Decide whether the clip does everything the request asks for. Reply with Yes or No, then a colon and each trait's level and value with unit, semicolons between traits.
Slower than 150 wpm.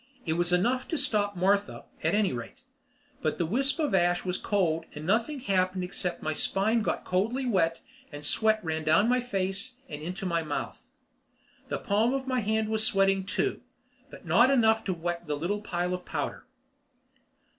No: average, 180 wpm